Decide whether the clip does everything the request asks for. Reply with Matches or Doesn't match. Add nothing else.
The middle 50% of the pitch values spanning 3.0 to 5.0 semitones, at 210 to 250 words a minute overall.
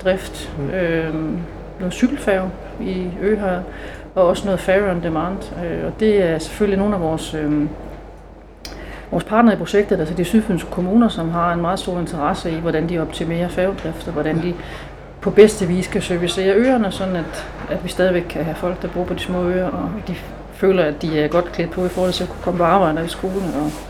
Doesn't match